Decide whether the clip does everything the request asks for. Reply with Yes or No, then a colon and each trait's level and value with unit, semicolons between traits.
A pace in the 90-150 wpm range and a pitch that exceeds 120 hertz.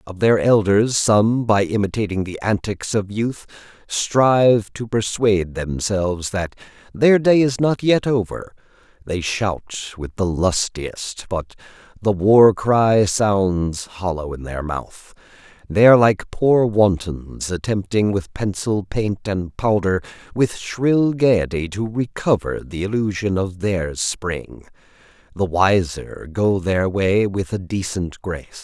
No: slow, 135 wpm; low, 100 Hz